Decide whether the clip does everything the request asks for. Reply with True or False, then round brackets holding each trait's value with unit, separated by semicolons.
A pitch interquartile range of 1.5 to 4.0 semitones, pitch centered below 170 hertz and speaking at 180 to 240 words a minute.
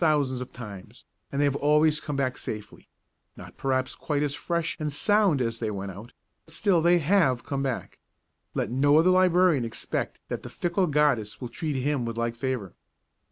False (4.8 semitones; 140 Hz; 185 wpm)